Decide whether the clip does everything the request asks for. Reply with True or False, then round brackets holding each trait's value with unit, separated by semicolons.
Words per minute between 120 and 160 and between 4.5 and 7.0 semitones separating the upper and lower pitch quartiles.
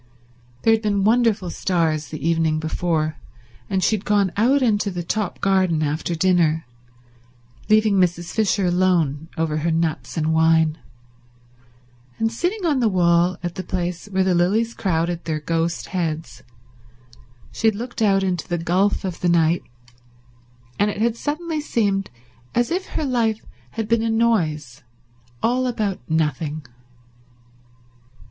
True (145 wpm; 5.1 semitones)